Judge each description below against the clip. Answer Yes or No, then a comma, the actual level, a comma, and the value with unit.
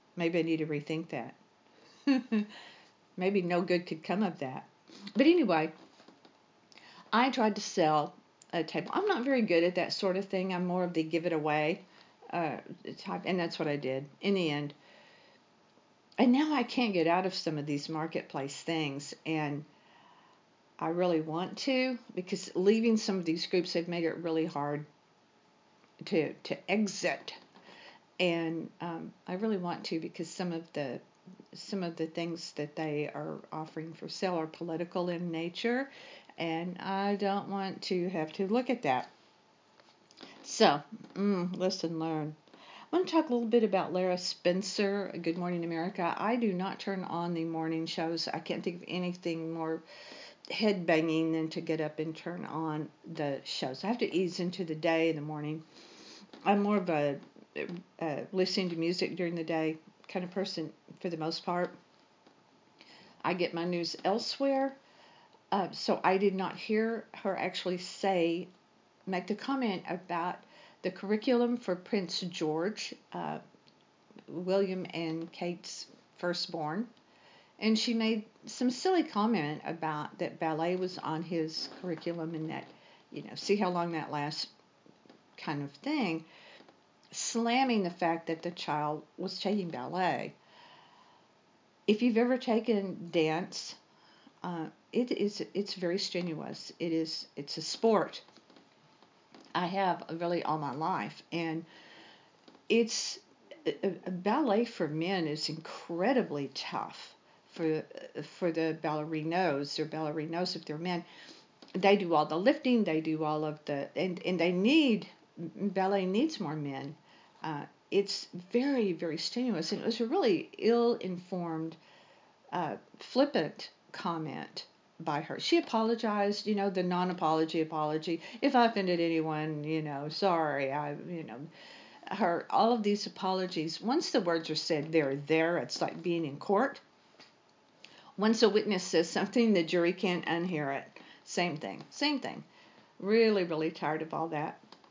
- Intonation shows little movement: No, average, 4.2 semitones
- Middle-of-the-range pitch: Yes, medium, 175 Hz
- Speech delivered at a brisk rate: No, average, 155 wpm